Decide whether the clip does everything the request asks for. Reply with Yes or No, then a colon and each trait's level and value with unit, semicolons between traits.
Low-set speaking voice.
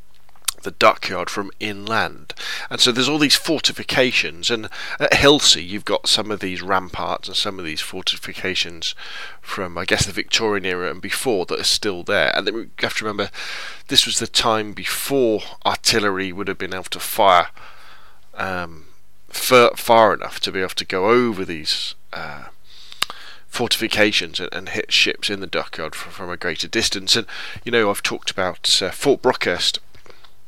Yes: low, 100 Hz